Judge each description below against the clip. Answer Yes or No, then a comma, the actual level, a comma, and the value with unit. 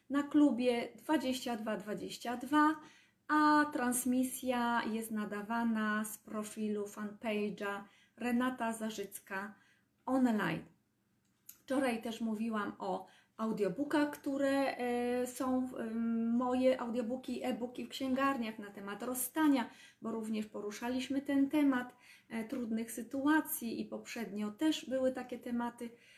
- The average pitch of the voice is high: Yes, high, 245 Hz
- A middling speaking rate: No, slow, 95 wpm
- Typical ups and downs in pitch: Yes, average, 3.0 semitones